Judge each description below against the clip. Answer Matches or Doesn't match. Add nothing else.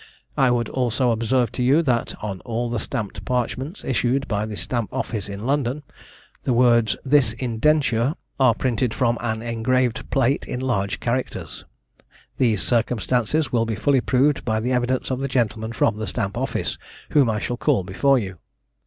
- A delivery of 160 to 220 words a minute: Matches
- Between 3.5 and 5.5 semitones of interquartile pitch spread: Doesn't match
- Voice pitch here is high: Doesn't match